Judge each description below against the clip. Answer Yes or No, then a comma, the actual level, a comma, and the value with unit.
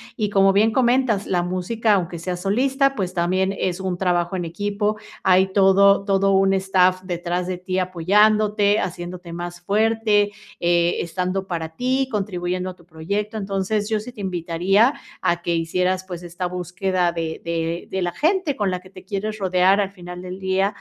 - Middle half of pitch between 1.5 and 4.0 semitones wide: Yes, narrow, 2.6 semitones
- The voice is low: No, high, 190 Hz